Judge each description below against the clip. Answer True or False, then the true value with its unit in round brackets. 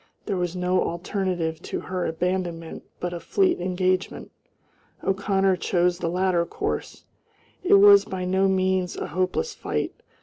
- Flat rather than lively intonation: True (1.4 semitones)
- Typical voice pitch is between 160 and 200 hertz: True (185 Hz)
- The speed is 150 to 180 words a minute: False (140 wpm)